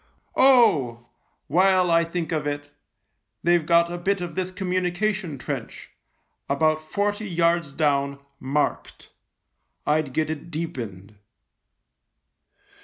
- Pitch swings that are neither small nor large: Yes, average, 3.9 semitones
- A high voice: No, medium, 165 Hz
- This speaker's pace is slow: Yes, slow, 110 wpm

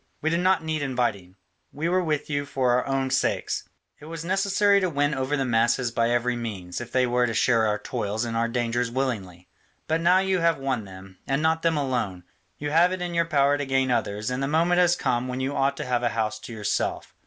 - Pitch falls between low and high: No, low, 130 Hz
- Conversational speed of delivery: No, fast, 235 wpm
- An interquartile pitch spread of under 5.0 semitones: No, average, 5.3 semitones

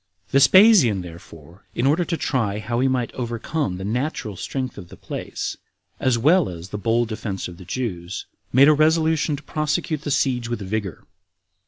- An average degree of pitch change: No, wide, 6.5 semitones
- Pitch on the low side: Yes, low, 120 Hz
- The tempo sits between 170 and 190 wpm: Yes, average, 180 wpm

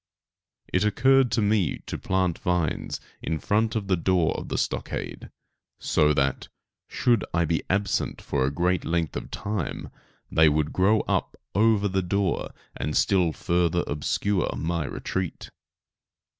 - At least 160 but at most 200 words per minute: No, average, 145 wpm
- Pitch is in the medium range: No, very low, 90 Hz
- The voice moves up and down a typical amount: Yes, average, 3.9 semitones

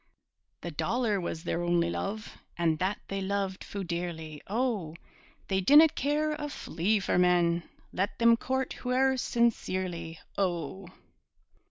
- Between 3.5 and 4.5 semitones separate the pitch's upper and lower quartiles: No, wide, 5.4 semitones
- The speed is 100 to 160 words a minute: Yes, slow, 135 wpm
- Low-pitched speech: No, high, 190 Hz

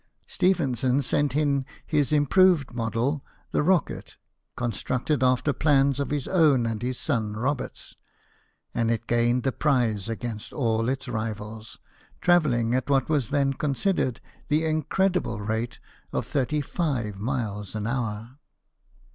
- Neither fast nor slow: No, slow, 130 wpm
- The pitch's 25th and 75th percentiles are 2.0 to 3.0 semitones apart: No, average, 4.2 semitones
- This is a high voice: No, low, 130 Hz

